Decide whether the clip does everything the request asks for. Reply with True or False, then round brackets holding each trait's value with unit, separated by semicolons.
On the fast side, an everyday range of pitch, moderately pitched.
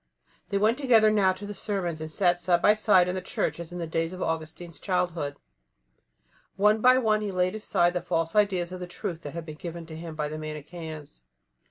True (220 wpm; 3.8 semitones; 175 Hz)